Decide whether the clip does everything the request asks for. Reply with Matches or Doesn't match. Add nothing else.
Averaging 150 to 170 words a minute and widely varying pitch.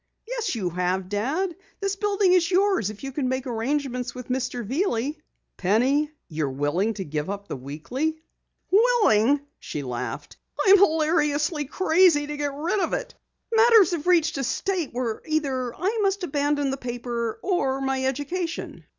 Matches